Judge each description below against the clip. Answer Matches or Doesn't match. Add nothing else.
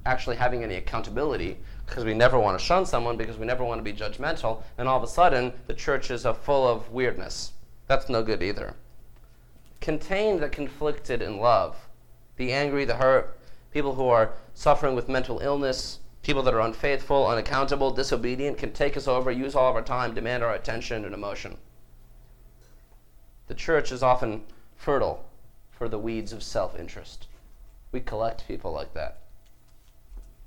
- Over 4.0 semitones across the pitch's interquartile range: Doesn't match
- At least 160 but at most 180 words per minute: Matches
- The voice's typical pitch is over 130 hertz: Doesn't match